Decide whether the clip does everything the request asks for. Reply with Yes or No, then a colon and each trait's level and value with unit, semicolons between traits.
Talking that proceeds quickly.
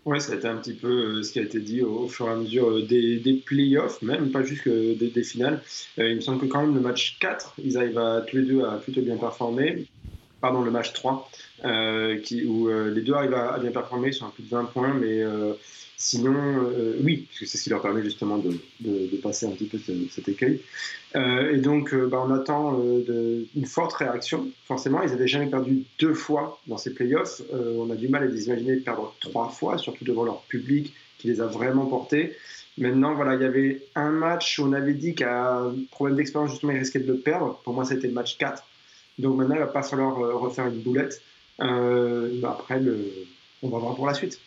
Yes: fast, 245 wpm